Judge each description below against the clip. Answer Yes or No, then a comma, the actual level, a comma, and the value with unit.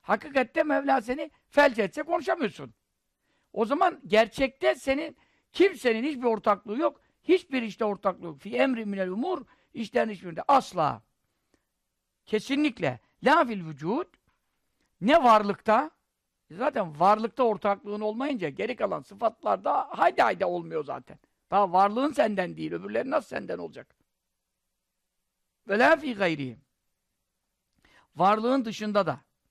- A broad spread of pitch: Yes, wide, 6.1 semitones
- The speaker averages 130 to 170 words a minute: No, average, 120 wpm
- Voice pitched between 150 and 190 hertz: No, high, 230 Hz